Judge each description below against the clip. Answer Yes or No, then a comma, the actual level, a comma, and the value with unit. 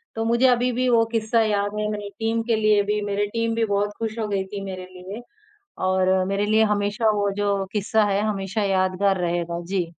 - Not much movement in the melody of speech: Yes, narrow, 2.3 semitones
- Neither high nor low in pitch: No, high, 205 Hz